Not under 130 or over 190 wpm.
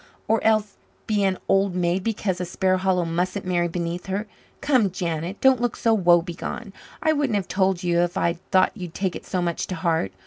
No: average, 200 wpm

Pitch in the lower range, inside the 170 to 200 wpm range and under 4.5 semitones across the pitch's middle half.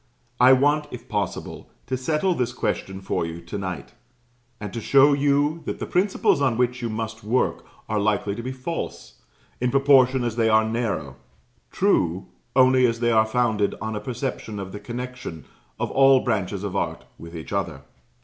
Yes: low, 120 Hz; average, 180 wpm; average, 4.1 semitones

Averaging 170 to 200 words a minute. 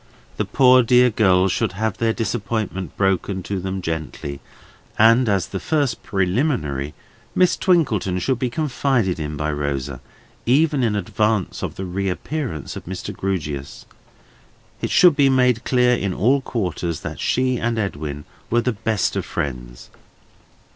No: average, 145 wpm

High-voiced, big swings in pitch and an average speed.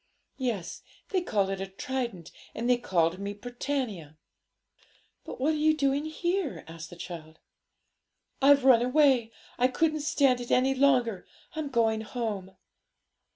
Yes: high, 245 Hz; wide, 6.3 semitones; average, 145 wpm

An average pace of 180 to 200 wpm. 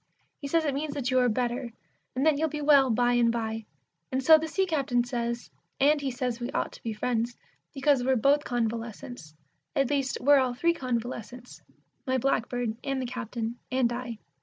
Yes: average, 195 wpm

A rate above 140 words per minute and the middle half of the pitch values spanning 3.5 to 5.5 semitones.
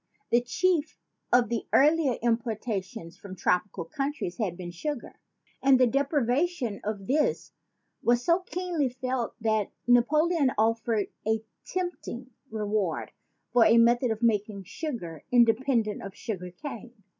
No: slow, 135 wpm; average, 4.4 semitones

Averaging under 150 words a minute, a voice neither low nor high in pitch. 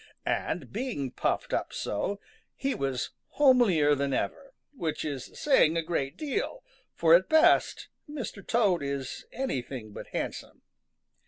Yes: slow, 135 wpm; medium, 170 Hz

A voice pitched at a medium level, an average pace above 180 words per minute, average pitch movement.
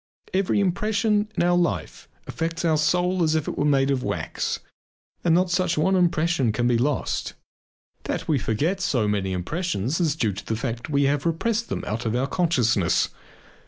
No: medium, 155 Hz; average, 190 wpm; wide, 6.5 semitones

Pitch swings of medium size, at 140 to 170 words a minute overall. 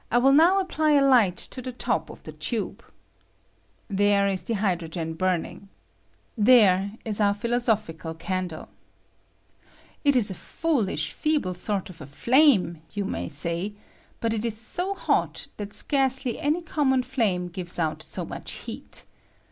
No: wide, 6.3 semitones; average, 155 wpm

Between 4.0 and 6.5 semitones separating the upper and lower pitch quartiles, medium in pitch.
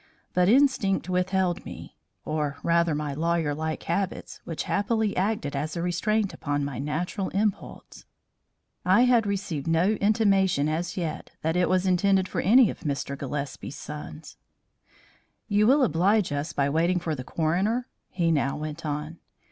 Yes: average, 4.6 semitones; medium, 175 Hz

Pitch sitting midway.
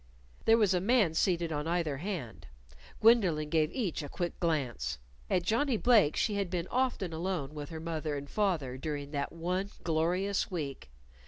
Yes: medium, 170 Hz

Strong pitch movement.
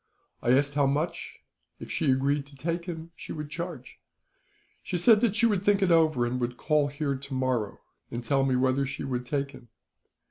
No: average, 4.2 semitones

